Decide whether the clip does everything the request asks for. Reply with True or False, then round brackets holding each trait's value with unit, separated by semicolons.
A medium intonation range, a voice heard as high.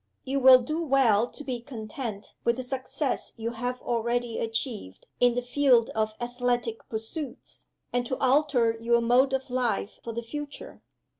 False (2.3 semitones; 245 Hz)